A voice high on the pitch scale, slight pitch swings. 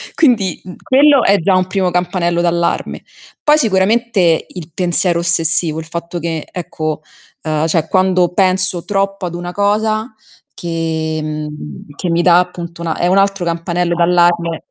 No: medium, 175 Hz; narrow, 2.3 semitones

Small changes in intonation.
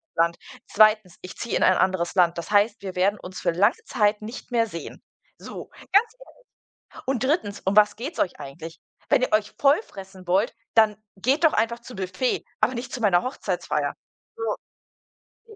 No: average, 4.4 semitones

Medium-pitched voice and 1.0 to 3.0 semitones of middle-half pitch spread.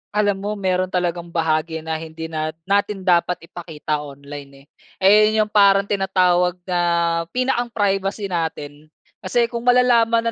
No: medium, 180 Hz; average, 4.2 semitones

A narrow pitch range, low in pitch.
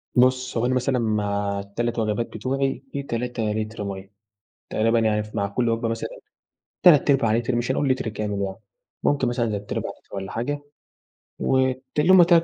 No: average, 3.5 semitones; low, 115 Hz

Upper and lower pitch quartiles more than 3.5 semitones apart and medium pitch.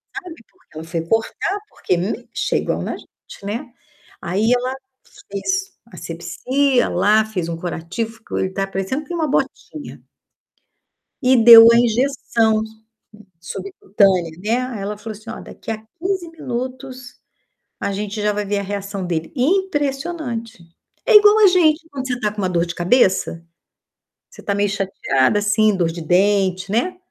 No: average, 5.3 semitones; high, 215 Hz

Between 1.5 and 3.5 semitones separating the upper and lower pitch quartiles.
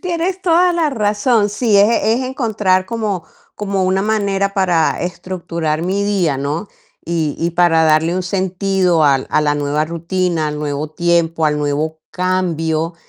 No: average, 4.3 semitones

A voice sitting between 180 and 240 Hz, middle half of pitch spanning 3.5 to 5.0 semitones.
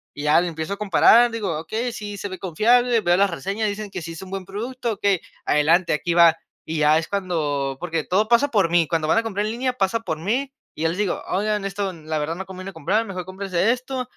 Yes: high, 190 Hz; average, 4.5 semitones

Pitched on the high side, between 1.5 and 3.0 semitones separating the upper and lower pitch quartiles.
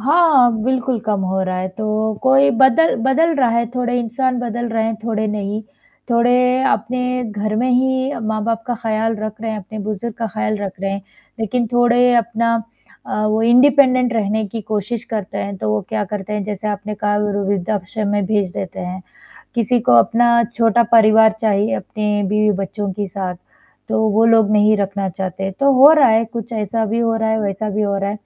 Yes: high, 220 Hz; narrow, 2.6 semitones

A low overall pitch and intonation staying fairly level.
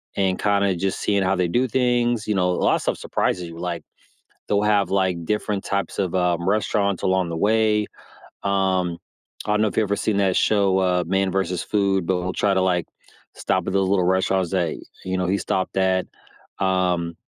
Yes: very low, 95 Hz; narrow, 1.9 semitones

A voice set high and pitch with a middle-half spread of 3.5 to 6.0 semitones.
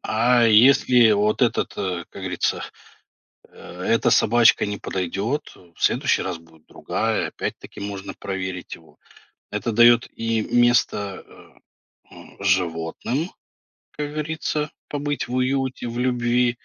No: low, 115 Hz; average, 4.5 semitones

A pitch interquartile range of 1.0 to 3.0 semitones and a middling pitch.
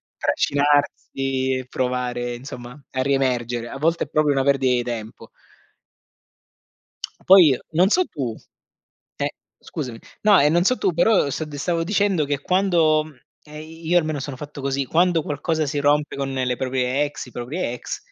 No: average, 3.6 semitones; medium, 145 Hz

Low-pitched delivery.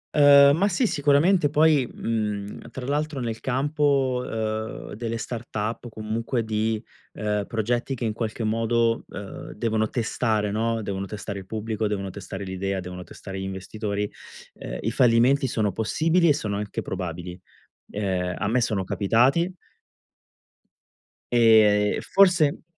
Yes: low, 110 Hz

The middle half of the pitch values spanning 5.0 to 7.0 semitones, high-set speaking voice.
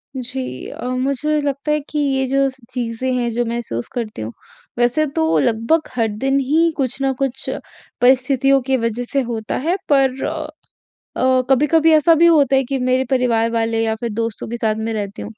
No: average, 3.0 semitones; very high, 255 Hz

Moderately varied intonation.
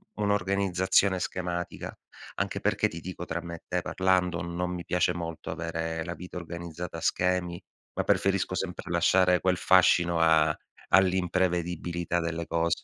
No: narrow, 1.5 semitones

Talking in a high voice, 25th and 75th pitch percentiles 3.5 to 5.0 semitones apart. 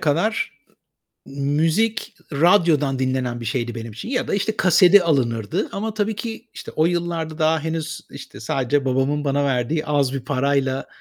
No: medium, 145 Hz; average, 4.6 semitones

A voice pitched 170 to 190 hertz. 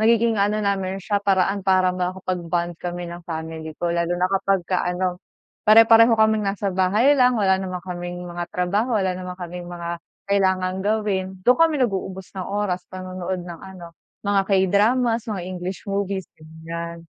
Yes: medium, 185 Hz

